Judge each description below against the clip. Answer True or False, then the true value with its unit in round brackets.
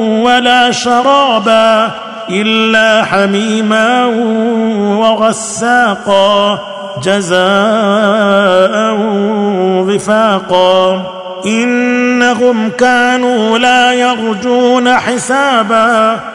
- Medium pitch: False (220 Hz)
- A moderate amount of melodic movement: True (3.3 semitones)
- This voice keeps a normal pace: False (45 wpm)